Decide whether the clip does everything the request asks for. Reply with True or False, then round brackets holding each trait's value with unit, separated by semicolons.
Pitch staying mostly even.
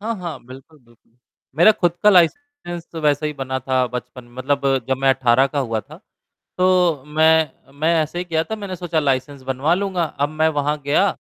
False (4.6 semitones)